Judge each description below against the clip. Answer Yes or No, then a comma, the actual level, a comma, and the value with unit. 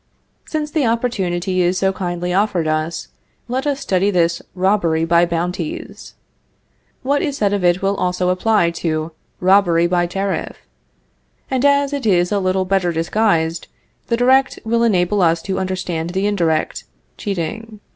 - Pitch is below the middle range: No, medium, 185 Hz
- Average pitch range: Yes, average, 4.0 semitones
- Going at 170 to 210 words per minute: No, average, 150 wpm